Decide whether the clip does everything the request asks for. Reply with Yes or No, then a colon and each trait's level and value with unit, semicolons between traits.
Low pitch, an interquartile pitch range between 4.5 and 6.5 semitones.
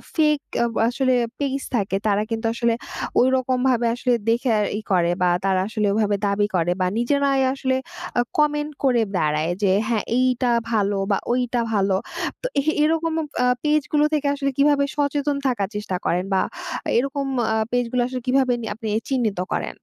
No: high, 245 Hz; average, 4.9 semitones